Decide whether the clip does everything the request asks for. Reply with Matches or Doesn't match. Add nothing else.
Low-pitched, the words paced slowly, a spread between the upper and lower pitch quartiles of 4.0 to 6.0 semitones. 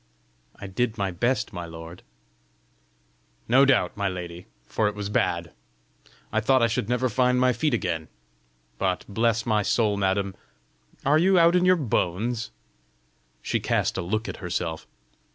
Doesn't match